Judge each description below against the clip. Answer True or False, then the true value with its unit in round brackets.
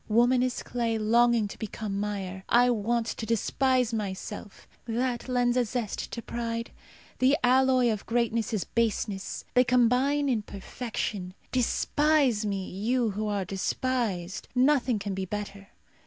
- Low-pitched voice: False (230 Hz)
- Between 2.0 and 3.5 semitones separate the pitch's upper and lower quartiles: True (3.2 semitones)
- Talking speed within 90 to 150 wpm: True (140 wpm)